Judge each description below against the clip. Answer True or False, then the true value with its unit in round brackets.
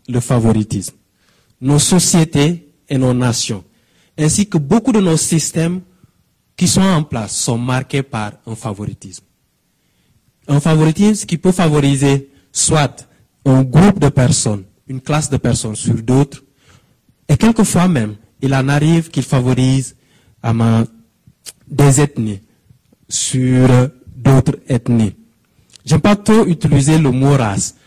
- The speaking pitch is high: False (135 Hz)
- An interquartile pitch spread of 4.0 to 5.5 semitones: True (4.7 semitones)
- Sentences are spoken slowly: True (125 wpm)